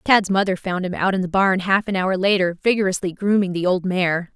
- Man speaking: No, female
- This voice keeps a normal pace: No, fast, 235 wpm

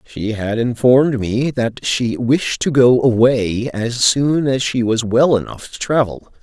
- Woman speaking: No, male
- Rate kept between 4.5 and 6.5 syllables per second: No, 3.9 syllables/s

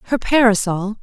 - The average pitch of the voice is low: No, high, 220 Hz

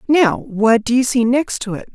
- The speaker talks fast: Yes, fast, 245 wpm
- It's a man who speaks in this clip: No, female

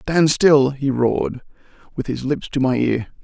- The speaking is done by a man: Yes, male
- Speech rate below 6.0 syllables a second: Yes, 4.2 syllables/s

